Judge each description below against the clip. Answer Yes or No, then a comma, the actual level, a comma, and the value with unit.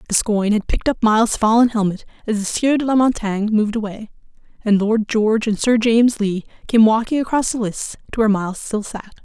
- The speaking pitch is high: Yes, high, 220 Hz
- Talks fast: Yes, fast, 210 wpm